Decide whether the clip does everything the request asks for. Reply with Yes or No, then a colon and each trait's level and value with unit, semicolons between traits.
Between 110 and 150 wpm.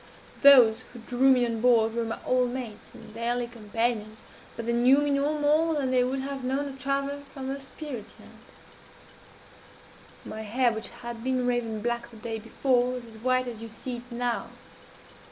No: average, 190 wpm